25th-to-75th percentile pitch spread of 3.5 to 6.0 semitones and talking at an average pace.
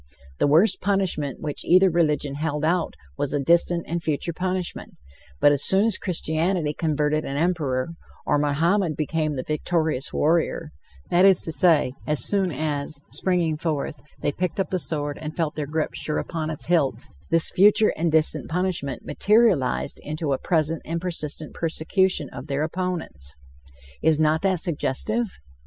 No: average, 3.1 semitones; average, 165 wpm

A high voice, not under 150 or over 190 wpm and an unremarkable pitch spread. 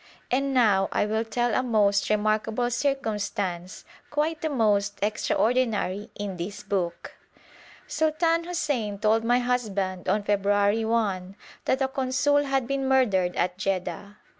No: high, 220 Hz; slow, 135 wpm; average, 4.4 semitones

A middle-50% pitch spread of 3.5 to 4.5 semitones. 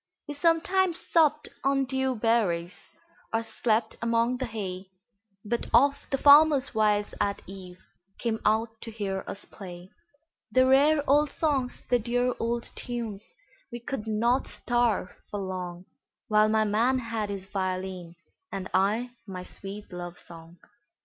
No: average, 4.9 semitones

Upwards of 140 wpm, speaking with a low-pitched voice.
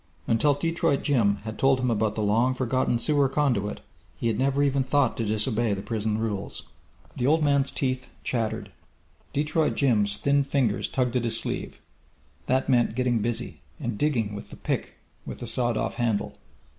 Yes: average, 175 wpm; low, 125 Hz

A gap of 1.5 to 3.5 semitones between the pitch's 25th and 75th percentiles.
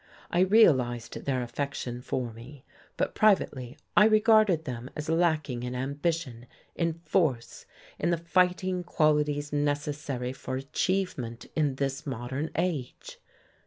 No: average, 5.0 semitones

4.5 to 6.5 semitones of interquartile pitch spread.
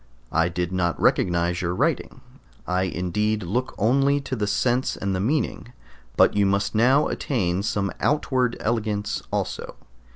Yes: average, 5.2 semitones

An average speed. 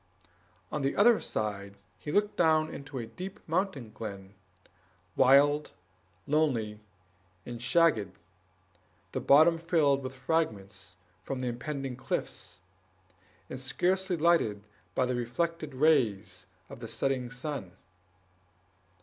No: slow, 115 wpm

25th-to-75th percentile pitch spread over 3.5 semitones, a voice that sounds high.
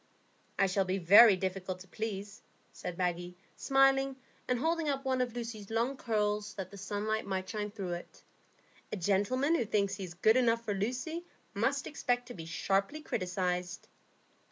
Yes: average, 4.6 semitones; high, 210 Hz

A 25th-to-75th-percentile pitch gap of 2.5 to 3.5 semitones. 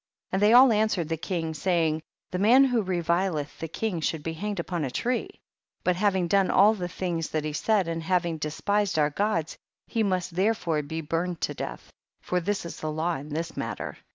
No: average, 3.9 semitones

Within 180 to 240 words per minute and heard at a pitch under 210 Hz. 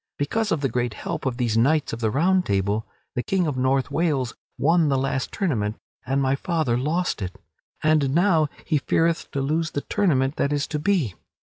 Yes: average, 200 wpm; medium, 140 Hz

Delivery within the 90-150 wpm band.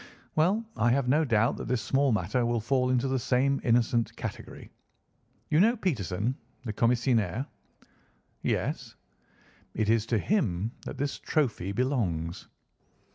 Yes: slow, 135 wpm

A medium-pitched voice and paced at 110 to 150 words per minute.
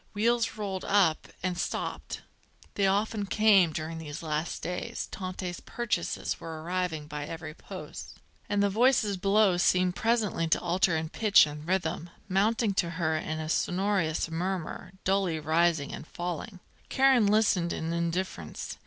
Yes: medium, 180 Hz; average, 145 wpm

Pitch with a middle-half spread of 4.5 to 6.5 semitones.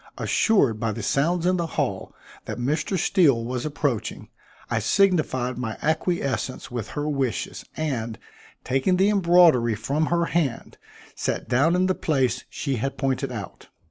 Yes: wide, 5.6 semitones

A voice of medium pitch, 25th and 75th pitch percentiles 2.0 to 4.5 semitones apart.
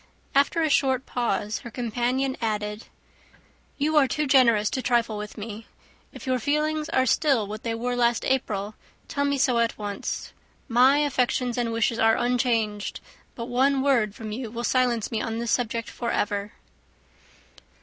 No: high, 240 Hz; average, 3.0 semitones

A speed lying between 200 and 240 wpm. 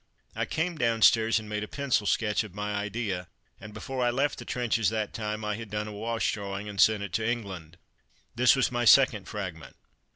Yes: fast, 205 wpm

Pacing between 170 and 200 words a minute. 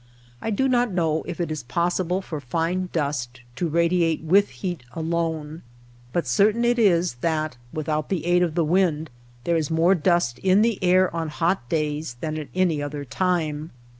Yes: average, 180 wpm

